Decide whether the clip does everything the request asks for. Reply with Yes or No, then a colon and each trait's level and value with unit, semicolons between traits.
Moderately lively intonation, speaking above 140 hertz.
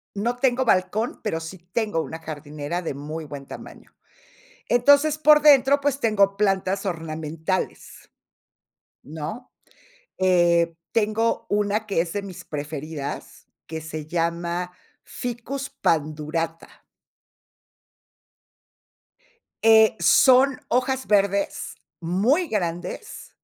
No: wide, 6.3 semitones; high, 190 Hz